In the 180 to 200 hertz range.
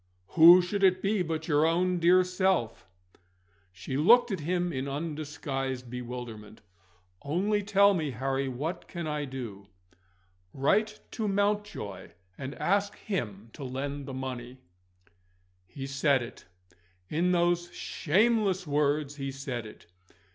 No: medium, 150 Hz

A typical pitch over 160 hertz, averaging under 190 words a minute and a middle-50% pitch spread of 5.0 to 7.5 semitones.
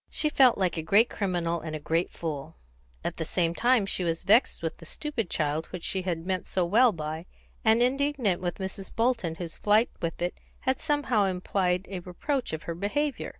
No: medium, 185 Hz; average, 200 wpm; wide, 5.6 semitones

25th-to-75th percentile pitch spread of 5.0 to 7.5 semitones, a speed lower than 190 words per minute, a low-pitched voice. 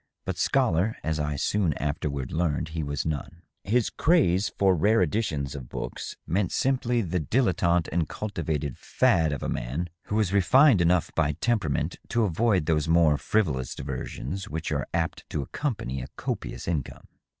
Yes: wide, 5.4 semitones; average, 165 wpm; very low, 85 Hz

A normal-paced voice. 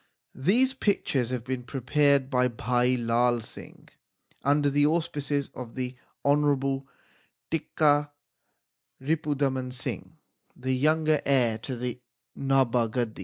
No: slow, 120 wpm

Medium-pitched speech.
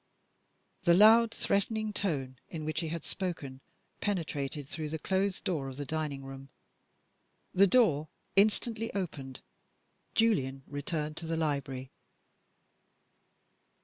Yes: medium, 160 Hz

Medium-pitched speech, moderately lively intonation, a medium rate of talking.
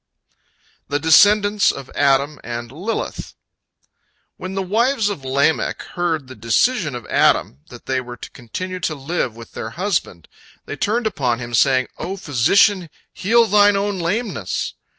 No: medium, 160 Hz; wide, 7.9 semitones; average, 150 wpm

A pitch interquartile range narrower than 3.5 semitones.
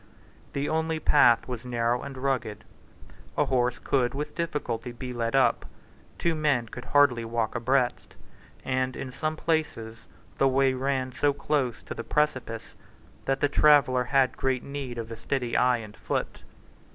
Yes: average, 2.8 semitones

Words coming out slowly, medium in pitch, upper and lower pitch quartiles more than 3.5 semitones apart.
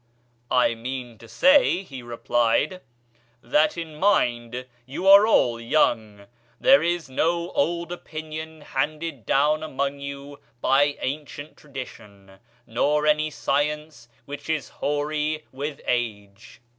Yes: slow, 120 wpm; medium, 145 Hz; average, 4.3 semitones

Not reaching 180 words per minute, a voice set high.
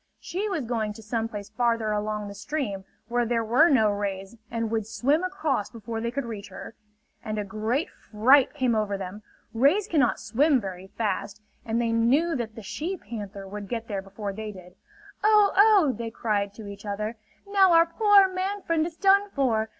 No: average, 195 wpm; high, 230 Hz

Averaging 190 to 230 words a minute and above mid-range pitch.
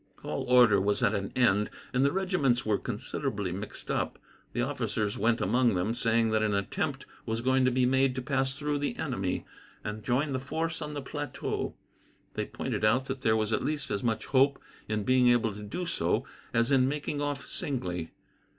No: average, 195 wpm; low, 125 Hz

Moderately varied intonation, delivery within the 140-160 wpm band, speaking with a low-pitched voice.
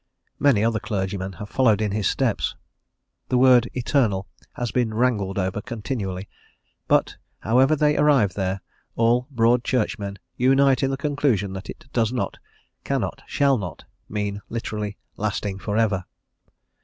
Yes: average, 4.1 semitones; average, 145 wpm; low, 110 Hz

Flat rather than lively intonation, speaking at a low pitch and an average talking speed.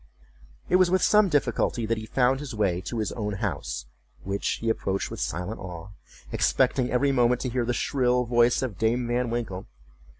No: average, 3.3 semitones; low, 120 Hz; average, 190 wpm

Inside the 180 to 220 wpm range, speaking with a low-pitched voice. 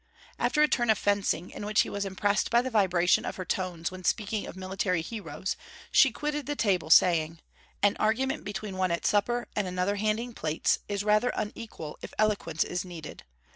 No: average, 190 wpm; high, 200 Hz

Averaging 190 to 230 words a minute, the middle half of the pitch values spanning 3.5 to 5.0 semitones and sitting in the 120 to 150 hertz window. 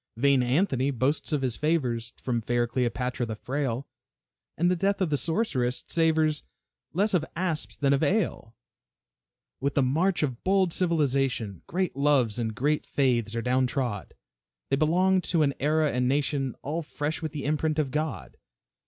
No: average, 165 wpm; average, 4.1 semitones; medium, 140 Hz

